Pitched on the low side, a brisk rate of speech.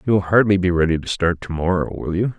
Yes: very low, 95 Hz; fast, 275 wpm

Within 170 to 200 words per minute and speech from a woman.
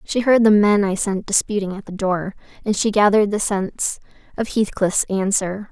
Yes: average, 190 wpm; female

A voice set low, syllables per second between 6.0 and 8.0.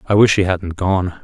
No: very low, 95 Hz; 4.9 syllables/s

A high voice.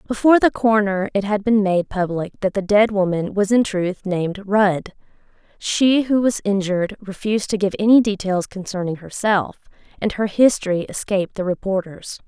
Yes: high, 200 Hz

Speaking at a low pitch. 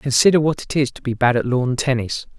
Yes: low, 130 Hz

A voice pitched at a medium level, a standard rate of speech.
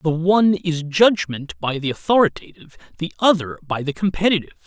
Yes: medium, 170 Hz; average, 165 wpm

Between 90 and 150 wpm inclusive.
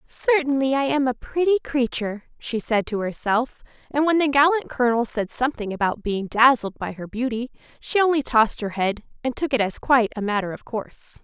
No: average, 200 wpm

